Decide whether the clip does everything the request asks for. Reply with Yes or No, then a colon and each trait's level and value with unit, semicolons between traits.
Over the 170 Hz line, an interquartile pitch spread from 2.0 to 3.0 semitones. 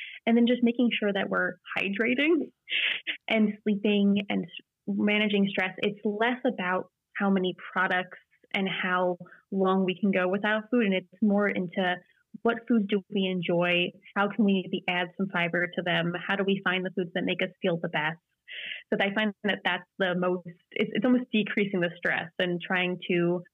Yes: high, 190 Hz; average, 2.7 semitones